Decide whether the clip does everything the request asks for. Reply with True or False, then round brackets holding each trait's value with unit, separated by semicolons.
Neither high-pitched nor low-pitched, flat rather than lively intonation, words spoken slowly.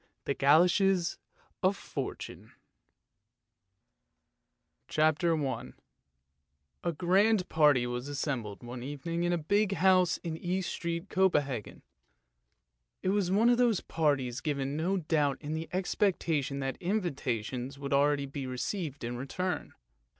False (155 Hz; 5.0 semitones; 120 wpm)